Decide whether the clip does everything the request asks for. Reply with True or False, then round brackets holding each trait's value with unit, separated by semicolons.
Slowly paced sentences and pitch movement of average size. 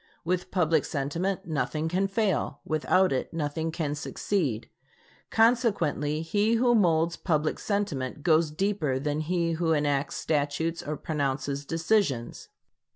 True (125 wpm; 4.1 semitones)